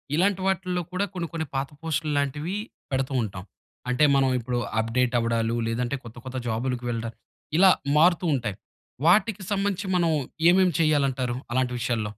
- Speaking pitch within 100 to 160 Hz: Yes, low, 135 Hz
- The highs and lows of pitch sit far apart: Yes, wide, 6.6 semitones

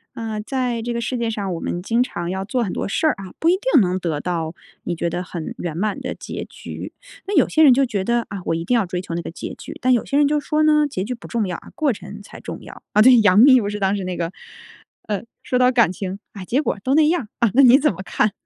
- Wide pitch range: Yes, wide, 5.7 semitones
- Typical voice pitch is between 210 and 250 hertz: Yes, high, 215 Hz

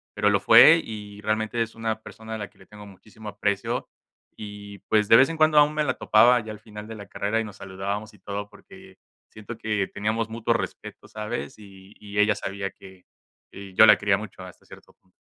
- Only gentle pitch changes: Yes, narrow, 1.8 semitones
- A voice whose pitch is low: Yes, low, 105 Hz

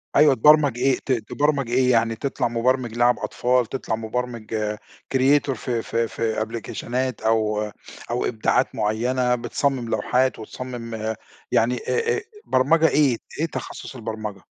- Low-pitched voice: Yes, low, 120 Hz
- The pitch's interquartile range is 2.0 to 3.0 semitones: Yes, average, 2.7 semitones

